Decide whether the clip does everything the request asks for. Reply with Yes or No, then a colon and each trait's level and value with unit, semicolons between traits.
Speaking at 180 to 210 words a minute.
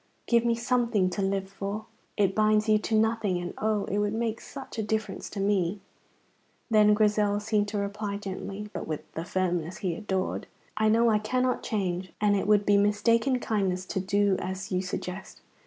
Yes: average, 190 wpm